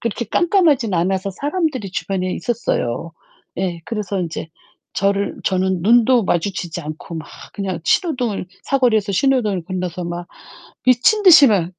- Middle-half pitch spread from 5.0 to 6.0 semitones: Yes, wide, 5.4 semitones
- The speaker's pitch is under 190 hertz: No, high, 200 Hz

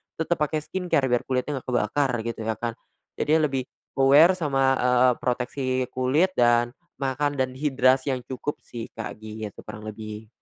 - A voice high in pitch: No, low, 130 Hz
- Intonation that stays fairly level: No, average, 3.3 semitones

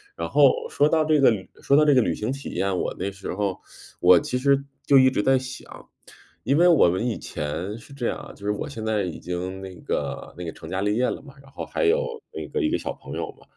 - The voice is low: Yes, low, 125 Hz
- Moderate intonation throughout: No, wide, 6.7 semitones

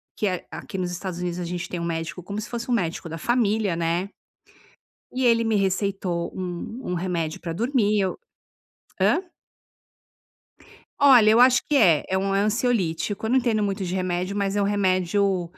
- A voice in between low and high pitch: No, high, 195 Hz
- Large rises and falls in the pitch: No, average, 3.7 semitones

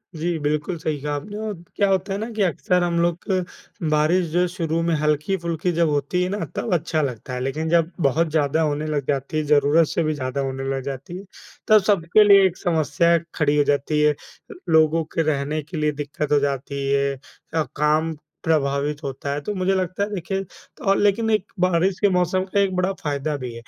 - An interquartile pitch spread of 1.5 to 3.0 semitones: No, average, 3.8 semitones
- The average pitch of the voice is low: No, medium, 160 Hz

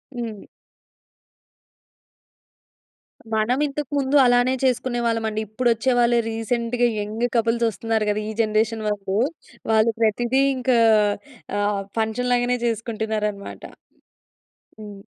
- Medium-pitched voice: No, high, 230 Hz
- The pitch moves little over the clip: Yes, narrow, 2.2 semitones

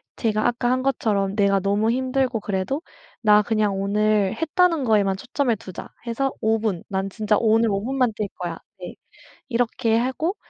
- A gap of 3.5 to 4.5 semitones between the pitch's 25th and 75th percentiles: Yes, average, 4.0 semitones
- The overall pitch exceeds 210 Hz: Yes, high, 220 Hz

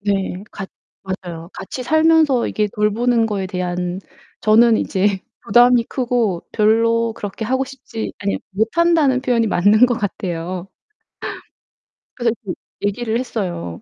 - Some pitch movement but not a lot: Yes, average, 4.1 semitones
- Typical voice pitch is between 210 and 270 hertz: Yes, high, 220 Hz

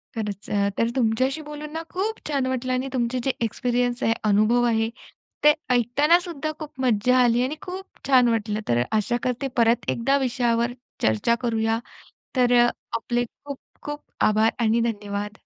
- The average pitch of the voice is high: Yes, high, 240 Hz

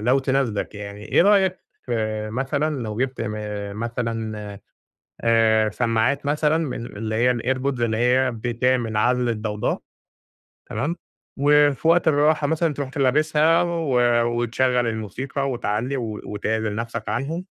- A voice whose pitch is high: No, low, 125 Hz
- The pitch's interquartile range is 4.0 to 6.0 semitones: Yes, average, 4.3 semitones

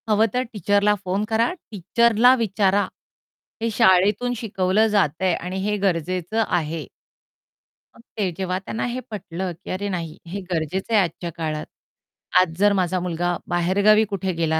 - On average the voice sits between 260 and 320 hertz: No, high, 190 Hz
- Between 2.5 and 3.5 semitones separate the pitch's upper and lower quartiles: Yes, average, 3.2 semitones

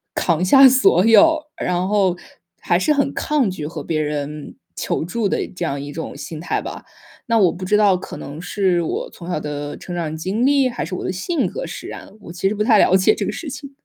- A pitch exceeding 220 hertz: No, medium, 185 Hz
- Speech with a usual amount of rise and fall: No, wide, 5.8 semitones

